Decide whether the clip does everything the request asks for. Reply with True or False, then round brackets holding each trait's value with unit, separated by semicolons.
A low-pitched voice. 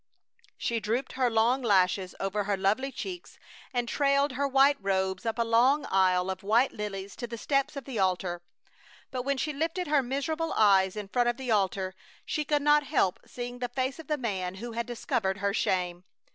False (235 Hz)